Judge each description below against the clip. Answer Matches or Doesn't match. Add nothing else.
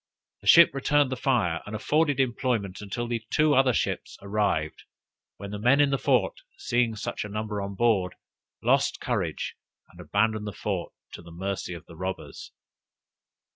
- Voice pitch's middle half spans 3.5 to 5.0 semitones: Matches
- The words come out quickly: Doesn't match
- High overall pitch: Doesn't match